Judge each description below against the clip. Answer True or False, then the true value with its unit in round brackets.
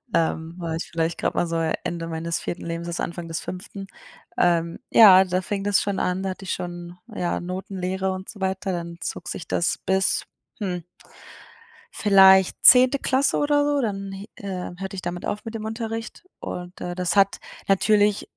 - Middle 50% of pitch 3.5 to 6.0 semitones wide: False (2.6 semitones)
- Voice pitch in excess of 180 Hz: True (190 Hz)